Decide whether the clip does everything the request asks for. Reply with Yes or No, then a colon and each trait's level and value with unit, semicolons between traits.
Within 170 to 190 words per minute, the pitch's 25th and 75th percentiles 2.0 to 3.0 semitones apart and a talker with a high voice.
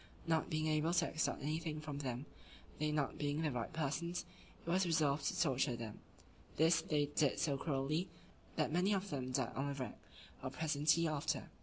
No: average, 185 wpm; narrow, 2.6 semitones; medium, 150 Hz